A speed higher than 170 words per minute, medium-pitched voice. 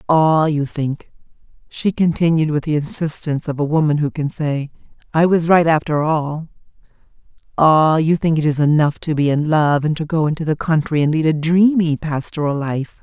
Yes: average, 190 wpm; medium, 155 Hz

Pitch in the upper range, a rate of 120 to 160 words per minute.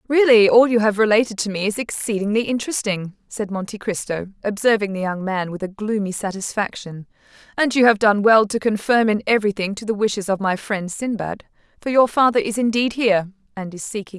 No: high, 210 Hz; average, 200 wpm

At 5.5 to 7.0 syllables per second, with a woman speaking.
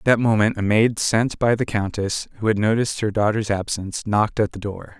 No: 5.7 syllables/s; male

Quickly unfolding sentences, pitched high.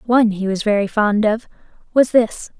No: average, 185 wpm; high, 220 Hz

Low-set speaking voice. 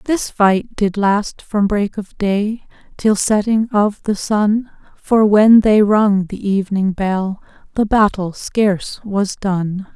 No: high, 205 Hz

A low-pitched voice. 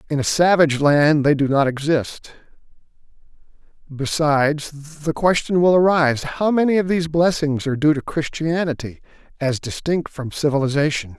No: medium, 150 Hz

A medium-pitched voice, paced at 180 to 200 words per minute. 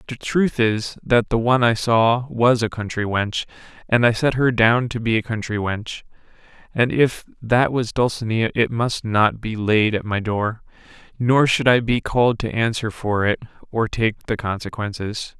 No: low, 115 Hz; average, 185 wpm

